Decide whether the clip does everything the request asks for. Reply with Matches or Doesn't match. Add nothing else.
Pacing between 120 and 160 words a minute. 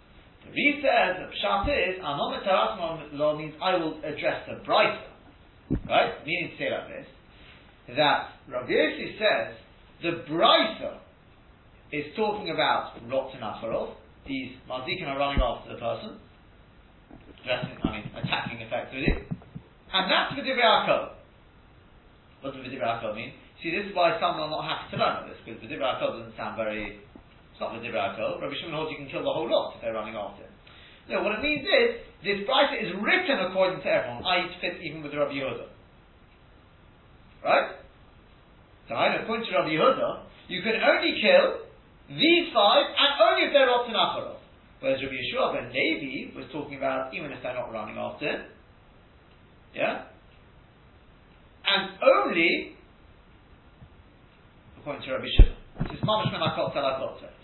Matches